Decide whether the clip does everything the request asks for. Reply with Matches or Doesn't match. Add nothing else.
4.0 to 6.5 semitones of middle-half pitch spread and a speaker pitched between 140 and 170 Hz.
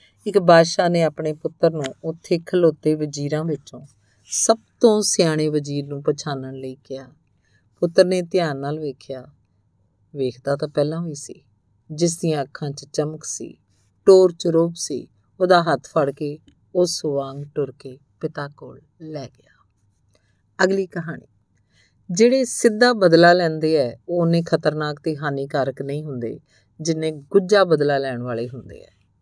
Matches